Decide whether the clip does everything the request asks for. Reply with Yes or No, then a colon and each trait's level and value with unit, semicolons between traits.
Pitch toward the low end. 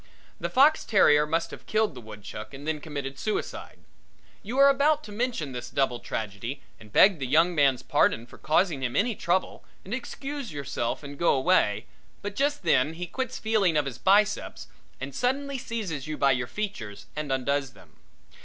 No: medium, 155 Hz